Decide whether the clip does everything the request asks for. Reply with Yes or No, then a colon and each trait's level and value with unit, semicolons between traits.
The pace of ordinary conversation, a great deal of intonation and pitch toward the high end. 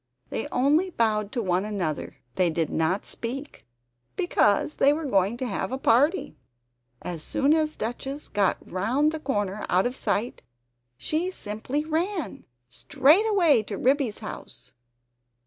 Yes: average, 145 wpm; wide, 6.9 semitones; high, 240 Hz